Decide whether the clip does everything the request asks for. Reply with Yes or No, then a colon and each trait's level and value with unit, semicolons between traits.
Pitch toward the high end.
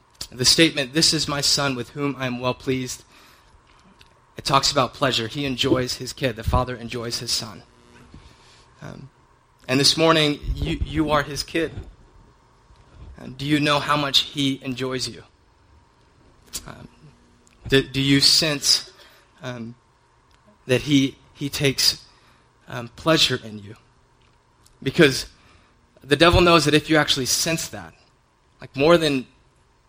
No: low, 135 Hz